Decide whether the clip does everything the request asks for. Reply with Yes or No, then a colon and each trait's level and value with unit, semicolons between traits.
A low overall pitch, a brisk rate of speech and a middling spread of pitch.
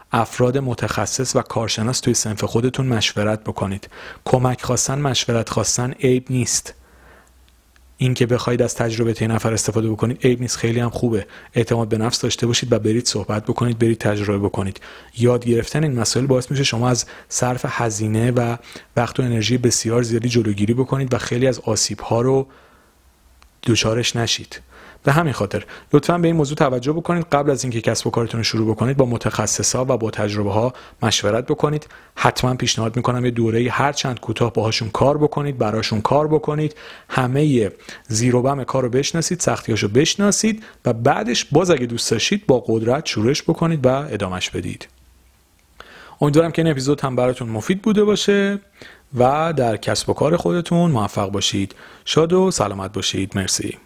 Yes: low, 120 Hz; fast, 165 wpm; average, 3.4 semitones